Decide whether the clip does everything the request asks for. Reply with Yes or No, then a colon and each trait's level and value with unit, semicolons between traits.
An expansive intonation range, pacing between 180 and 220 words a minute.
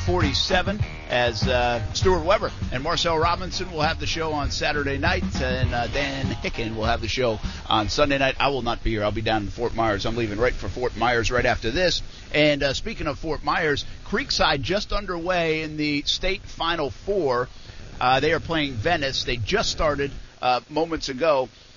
Yes: wide, 5.7 semitones; average, 195 wpm